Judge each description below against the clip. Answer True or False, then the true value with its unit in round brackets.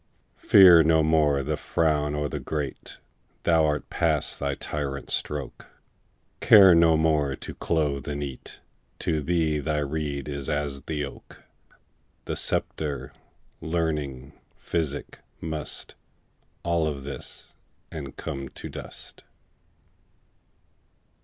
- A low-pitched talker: True (75 Hz)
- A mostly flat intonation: True (2.1 semitones)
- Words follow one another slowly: True (115 wpm)